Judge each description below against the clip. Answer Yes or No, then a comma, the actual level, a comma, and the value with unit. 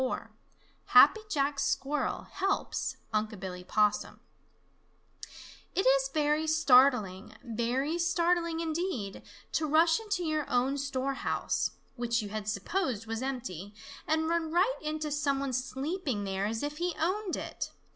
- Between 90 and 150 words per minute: Yes, slow, 135 wpm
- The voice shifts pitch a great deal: Yes, wide, 5.9 semitones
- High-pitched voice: Yes, very high, 275 Hz